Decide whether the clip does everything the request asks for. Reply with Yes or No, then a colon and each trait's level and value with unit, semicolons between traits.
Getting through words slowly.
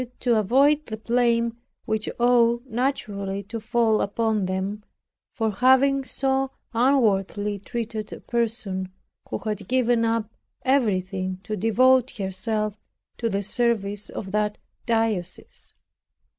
Yes: slow, 115 wpm